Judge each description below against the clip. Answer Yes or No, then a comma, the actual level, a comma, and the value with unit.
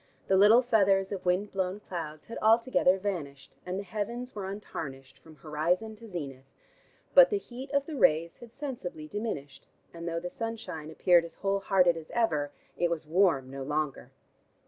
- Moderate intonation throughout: No, wide, 5.7 semitones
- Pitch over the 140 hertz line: Yes, medium, 185 Hz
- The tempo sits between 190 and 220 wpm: No, average, 175 wpm